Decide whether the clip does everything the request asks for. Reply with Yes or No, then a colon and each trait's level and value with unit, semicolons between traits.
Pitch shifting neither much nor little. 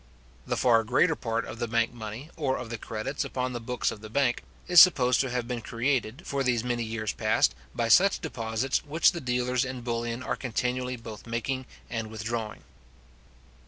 No: narrow, 2.2 semitones